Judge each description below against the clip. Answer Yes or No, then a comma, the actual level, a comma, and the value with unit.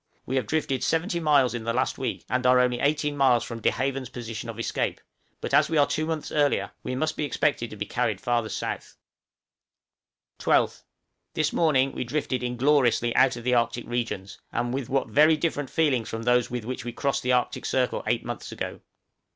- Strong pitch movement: No, average, 3.2 semitones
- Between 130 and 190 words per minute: No, average, 200 wpm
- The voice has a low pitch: Yes, low, 130 Hz